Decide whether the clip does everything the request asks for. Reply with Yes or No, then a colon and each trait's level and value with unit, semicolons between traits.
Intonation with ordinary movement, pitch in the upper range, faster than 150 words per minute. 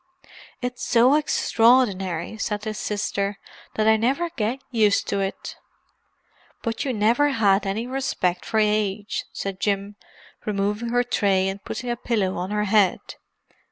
No: average, 3.2 semitones; high, 210 Hz; average, 145 wpm